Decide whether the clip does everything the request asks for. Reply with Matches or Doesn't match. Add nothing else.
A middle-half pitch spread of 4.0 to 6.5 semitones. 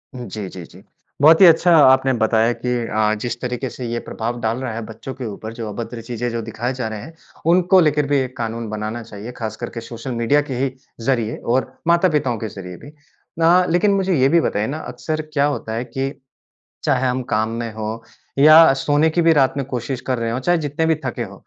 Matches